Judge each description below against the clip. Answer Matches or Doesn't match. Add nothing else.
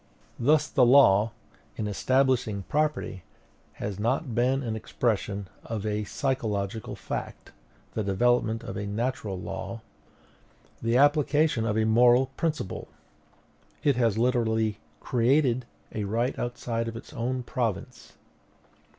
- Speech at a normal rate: Doesn't match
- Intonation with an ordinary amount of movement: Matches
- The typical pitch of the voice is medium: Doesn't match